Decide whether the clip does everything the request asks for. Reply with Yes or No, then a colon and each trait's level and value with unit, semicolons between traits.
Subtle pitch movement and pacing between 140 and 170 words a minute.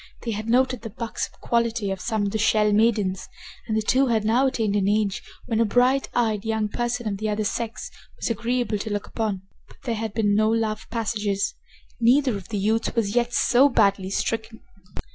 No: narrow, 2.1 semitones; average, 200 wpm